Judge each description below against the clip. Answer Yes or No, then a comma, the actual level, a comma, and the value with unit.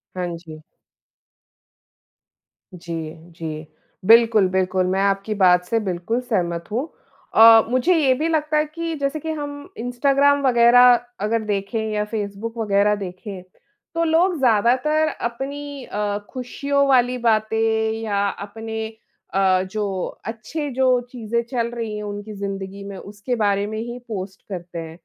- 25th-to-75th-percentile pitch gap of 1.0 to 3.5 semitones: No, average, 4.1 semitones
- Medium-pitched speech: No, high, 220 Hz